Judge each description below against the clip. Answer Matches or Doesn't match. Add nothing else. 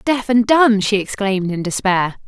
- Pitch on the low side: Doesn't match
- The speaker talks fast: Doesn't match